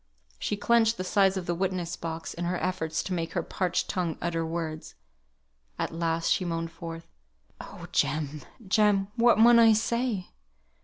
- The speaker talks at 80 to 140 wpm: No, average, 165 wpm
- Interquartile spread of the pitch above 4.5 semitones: No, average, 3.6 semitones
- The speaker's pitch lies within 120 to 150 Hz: No, medium, 180 Hz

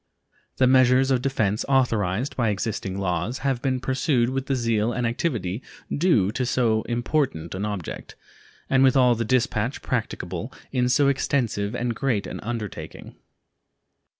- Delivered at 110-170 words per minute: Yes, average, 150 wpm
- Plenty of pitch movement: No, average, 3.9 semitones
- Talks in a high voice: No, low, 120 Hz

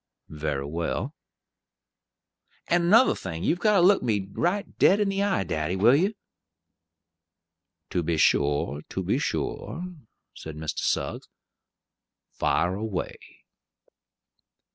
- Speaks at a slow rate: Yes, slow, 120 wpm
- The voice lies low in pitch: Yes, low, 100 Hz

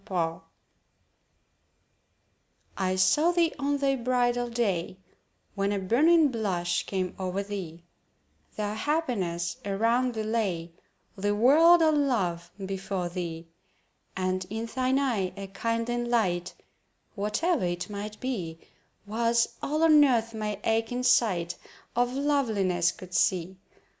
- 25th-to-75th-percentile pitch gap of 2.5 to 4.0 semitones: No, average, 5.1 semitones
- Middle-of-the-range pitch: No, high, 215 Hz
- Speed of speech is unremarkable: No, slow, 120 wpm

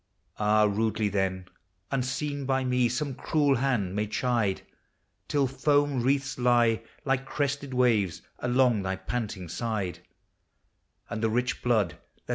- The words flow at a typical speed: No, slow, 130 wpm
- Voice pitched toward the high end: No, low, 120 Hz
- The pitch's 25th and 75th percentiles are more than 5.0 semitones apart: No, average, 4.0 semitones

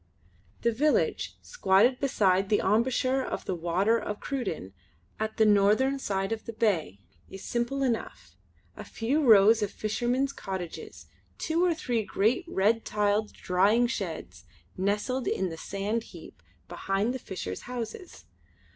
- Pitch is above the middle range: Yes, high, 215 Hz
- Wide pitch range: No, average, 4.2 semitones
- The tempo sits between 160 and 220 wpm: No, average, 140 wpm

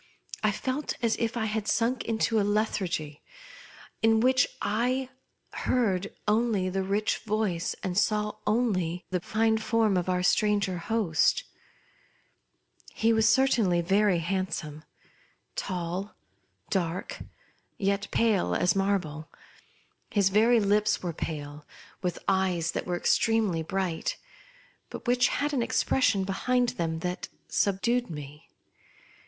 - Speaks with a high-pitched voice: Yes, high, 200 Hz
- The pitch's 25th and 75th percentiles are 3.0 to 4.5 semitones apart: Yes, average, 3.9 semitones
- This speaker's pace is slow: Yes, slow, 120 wpm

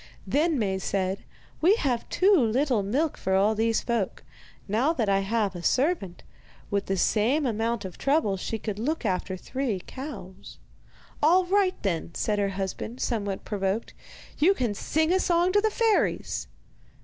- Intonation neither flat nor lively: No, wide, 7.6 semitones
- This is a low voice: No, high, 225 Hz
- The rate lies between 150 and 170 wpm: Yes, average, 160 wpm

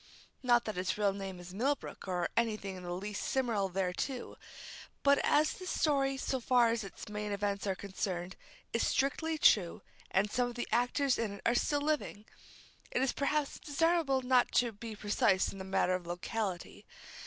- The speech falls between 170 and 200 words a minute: Yes, average, 190 wpm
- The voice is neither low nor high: No, high, 220 Hz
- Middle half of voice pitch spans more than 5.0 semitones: Yes, wide, 5.5 semitones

